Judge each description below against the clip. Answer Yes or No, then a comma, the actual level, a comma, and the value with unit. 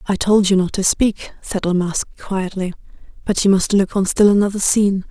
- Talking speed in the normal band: No, fast, 210 wpm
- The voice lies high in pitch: Yes, high, 195 Hz